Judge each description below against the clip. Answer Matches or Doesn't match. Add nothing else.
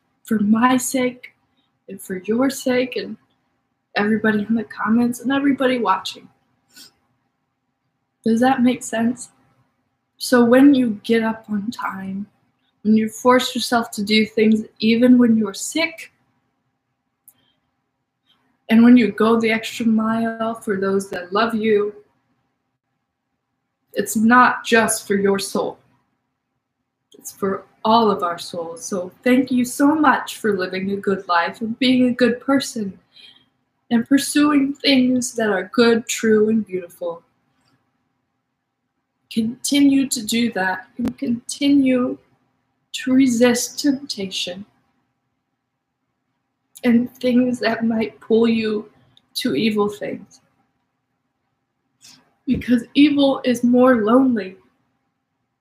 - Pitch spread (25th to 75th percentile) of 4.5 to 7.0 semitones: Matches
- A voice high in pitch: Matches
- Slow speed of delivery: Matches